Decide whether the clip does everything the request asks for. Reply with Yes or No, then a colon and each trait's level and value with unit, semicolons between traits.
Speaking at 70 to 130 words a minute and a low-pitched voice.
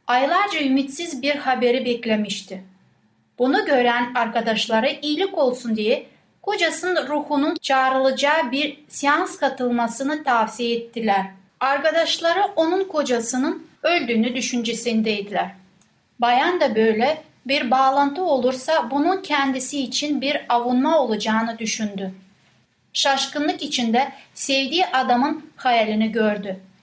No: slow, 95 wpm; very high, 260 Hz